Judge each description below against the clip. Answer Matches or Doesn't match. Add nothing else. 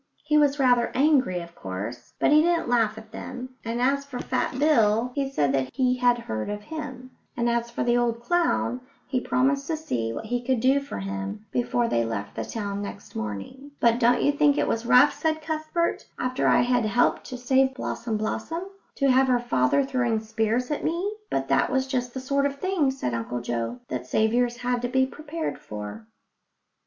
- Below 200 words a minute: Doesn't match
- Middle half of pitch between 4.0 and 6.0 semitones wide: Matches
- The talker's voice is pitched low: Doesn't match